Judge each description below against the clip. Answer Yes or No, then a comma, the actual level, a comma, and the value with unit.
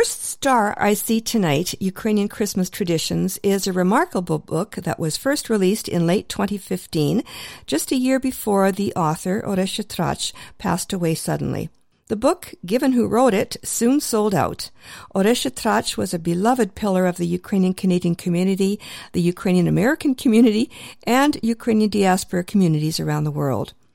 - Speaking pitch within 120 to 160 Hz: No, high, 200 Hz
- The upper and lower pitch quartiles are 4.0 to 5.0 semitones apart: Yes, average, 4.4 semitones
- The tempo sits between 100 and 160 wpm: Yes, average, 155 wpm